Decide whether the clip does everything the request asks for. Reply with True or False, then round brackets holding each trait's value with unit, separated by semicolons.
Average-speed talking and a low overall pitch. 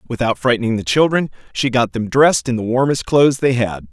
False (215 wpm; 125 Hz)